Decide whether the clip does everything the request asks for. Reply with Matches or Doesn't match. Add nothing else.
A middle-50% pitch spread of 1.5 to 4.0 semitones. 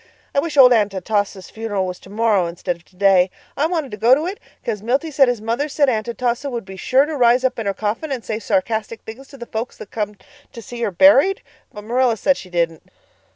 Doesn't match